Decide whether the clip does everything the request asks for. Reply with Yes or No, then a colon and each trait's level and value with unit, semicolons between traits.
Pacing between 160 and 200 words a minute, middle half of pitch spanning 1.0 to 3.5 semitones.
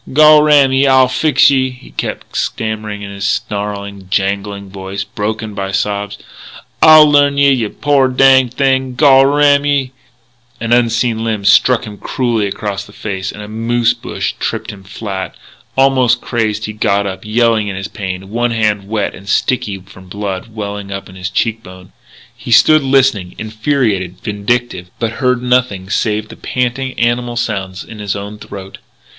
No: average, 170 wpm; average, 4.1 semitones